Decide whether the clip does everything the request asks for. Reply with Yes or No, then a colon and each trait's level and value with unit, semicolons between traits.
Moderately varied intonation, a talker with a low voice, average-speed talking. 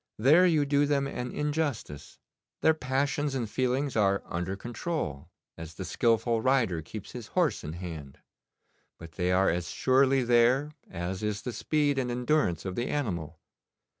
No: wide, 7.4 semitones; low, 120 Hz; average, 160 wpm